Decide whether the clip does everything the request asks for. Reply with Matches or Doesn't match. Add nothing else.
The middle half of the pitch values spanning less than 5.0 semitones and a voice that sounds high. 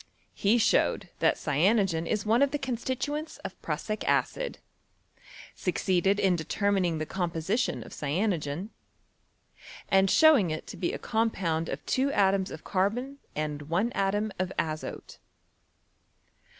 Doesn't match